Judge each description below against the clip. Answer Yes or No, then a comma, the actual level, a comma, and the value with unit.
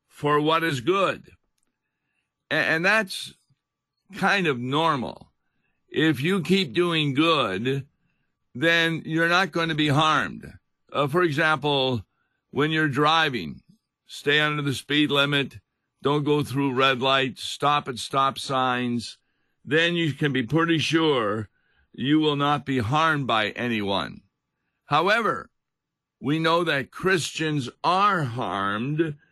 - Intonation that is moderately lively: Yes, average, 3.3 semitones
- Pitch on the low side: No, medium, 150 Hz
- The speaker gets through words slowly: Yes, slow, 125 wpm